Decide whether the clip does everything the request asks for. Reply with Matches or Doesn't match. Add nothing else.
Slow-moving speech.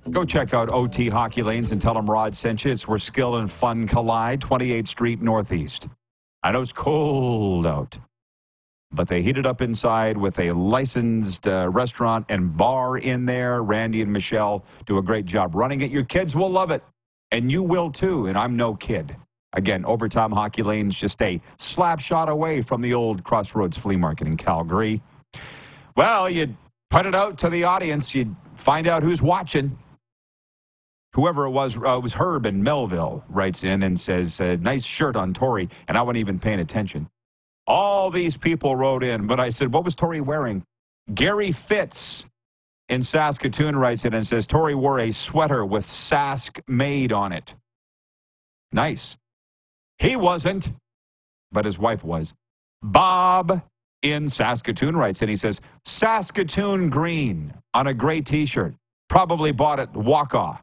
Doesn't match